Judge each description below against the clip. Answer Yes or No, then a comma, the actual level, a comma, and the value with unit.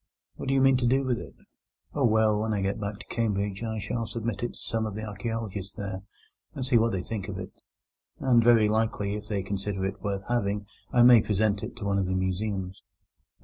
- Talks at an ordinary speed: No, fast, 230 wpm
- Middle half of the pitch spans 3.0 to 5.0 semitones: No, narrow, 2.6 semitones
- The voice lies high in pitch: No, low, 105 Hz